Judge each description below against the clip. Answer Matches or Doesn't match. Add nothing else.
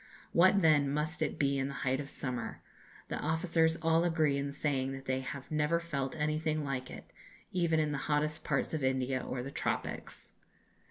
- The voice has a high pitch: Doesn't match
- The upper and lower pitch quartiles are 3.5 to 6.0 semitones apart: Doesn't match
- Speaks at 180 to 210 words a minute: Matches